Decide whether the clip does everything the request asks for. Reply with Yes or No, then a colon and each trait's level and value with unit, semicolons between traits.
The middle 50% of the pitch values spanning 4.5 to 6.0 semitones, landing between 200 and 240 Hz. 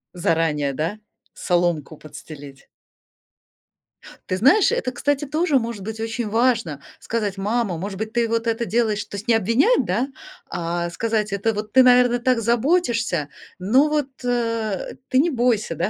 Yes: average, 4.9 semitones; high, 225 Hz